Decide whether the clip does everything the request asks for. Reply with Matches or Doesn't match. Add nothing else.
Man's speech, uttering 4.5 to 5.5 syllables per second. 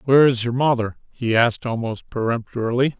Doesn't match